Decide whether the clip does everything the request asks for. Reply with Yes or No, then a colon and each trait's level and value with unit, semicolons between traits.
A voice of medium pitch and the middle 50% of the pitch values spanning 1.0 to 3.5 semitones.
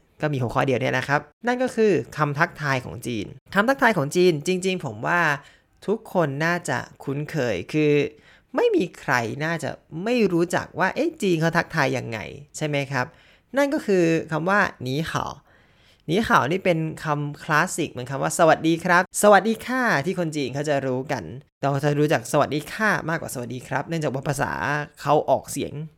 No: medium, 155 Hz; average, 4.4 semitones